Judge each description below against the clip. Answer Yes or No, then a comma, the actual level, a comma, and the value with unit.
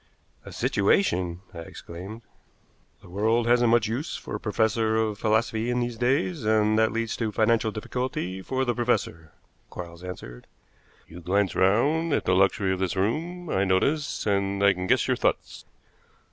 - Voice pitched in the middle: No, low, 110 Hz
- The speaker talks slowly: No, average, 165 wpm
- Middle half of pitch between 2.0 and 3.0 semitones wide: No, average, 4.2 semitones